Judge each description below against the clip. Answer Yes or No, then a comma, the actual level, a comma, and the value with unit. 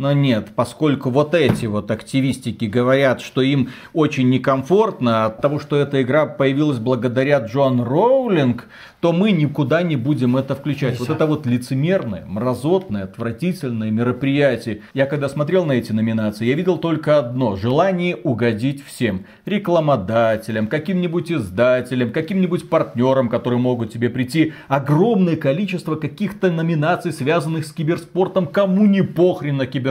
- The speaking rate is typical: Yes, average, 140 wpm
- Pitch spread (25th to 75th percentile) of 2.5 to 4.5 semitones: No, average, 4.9 semitones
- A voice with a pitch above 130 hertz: Yes, medium, 140 Hz